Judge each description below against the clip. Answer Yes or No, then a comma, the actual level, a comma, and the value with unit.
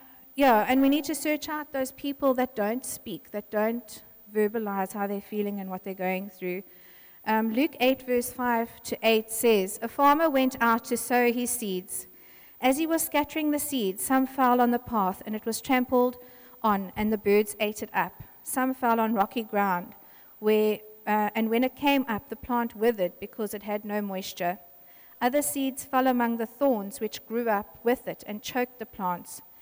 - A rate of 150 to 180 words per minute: No, average, 195 wpm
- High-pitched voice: Yes, high, 225 Hz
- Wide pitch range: No, average, 3.8 semitones